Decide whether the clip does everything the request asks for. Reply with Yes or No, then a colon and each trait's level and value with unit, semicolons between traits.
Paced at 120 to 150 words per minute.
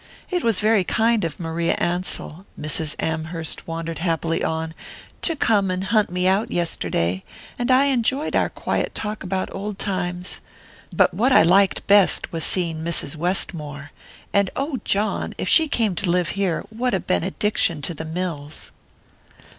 No: average, 160 wpm